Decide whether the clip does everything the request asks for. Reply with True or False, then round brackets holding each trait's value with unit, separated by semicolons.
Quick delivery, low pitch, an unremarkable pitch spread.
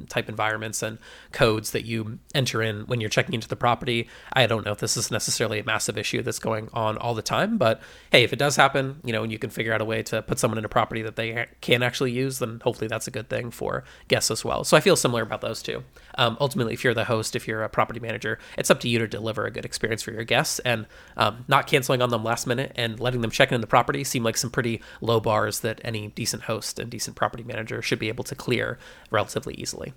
False (265 wpm; 115 Hz; 2.1 semitones)